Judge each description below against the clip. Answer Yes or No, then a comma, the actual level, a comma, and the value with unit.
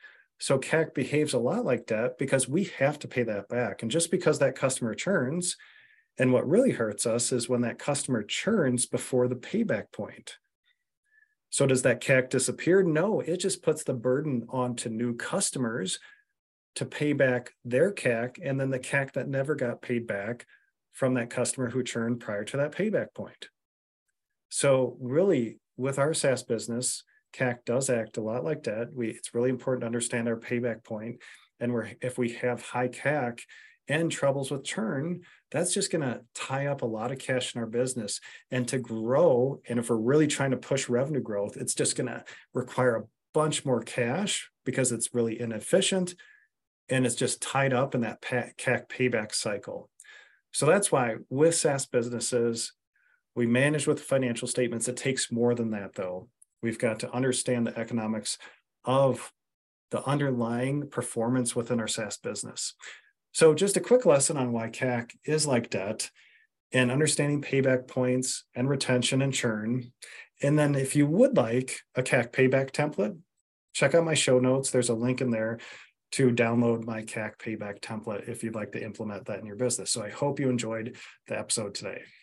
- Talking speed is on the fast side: No, average, 180 wpm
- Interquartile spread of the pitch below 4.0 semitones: Yes, average, 3.1 semitones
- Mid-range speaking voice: No, low, 125 Hz